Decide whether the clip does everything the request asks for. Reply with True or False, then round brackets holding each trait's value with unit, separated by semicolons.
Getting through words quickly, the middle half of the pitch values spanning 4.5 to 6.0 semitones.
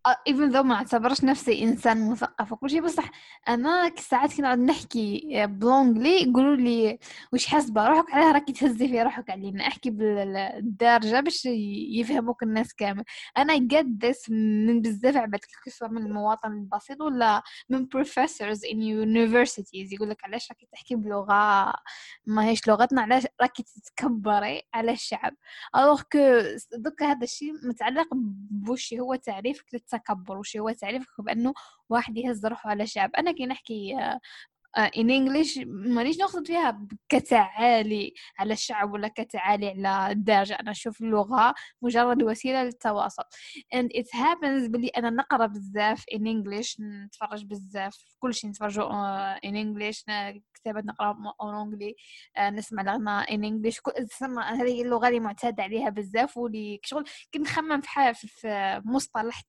False (140 wpm; 3.7 semitones)